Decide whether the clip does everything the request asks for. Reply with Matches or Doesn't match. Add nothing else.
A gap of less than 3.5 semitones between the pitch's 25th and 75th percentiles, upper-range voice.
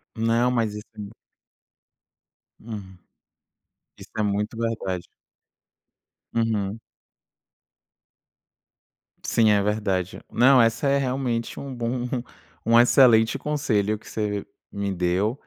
Doesn't match